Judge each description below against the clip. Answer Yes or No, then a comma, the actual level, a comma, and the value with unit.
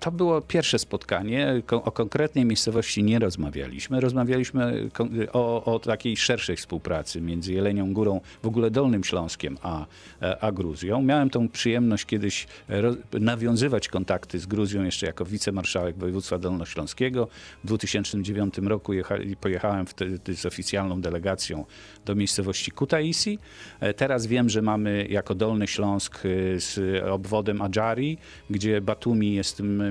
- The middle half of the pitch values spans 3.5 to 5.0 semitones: Yes, average, 3.8 semitones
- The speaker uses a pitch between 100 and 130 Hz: Yes, low, 105 Hz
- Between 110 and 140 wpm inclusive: Yes, average, 130 wpm